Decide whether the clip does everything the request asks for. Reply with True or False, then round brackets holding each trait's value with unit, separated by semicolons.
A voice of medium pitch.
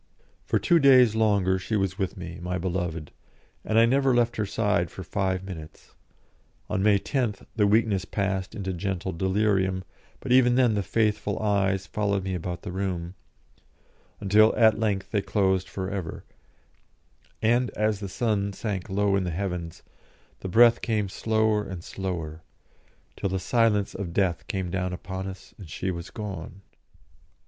False (100 Hz)